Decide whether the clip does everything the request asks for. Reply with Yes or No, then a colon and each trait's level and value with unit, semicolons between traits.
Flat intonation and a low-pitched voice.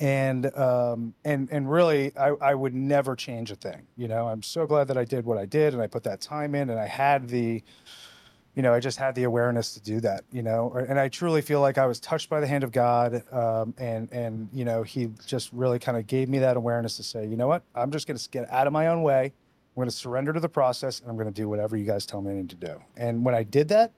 No: average, 3.2 semitones; low, 125 Hz